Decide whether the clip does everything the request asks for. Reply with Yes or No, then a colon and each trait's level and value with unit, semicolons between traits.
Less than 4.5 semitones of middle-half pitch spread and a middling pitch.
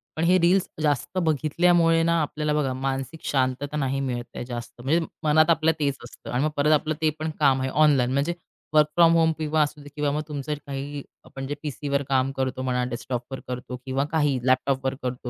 Yes: average, 2.8 semitones; medium, 145 Hz